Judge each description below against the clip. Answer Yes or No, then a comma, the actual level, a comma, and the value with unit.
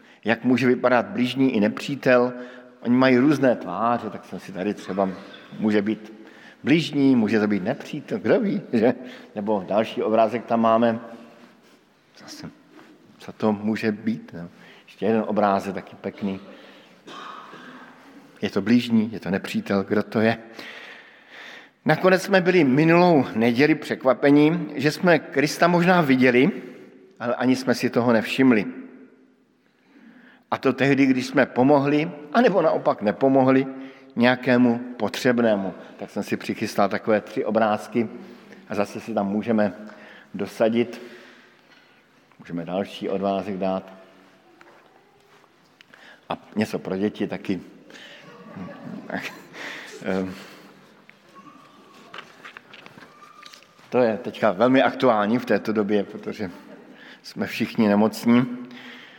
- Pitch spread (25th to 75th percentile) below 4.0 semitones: No, average, 4.4 semitones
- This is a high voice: No, low, 120 Hz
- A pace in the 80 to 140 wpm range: Yes, average, 115 wpm